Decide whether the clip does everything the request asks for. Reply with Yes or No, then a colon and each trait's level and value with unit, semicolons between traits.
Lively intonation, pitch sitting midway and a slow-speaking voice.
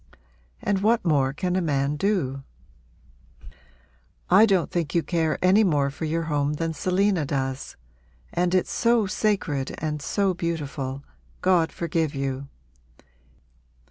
No: average, 4.6 semitones; medium, 165 Hz; slow, 130 wpm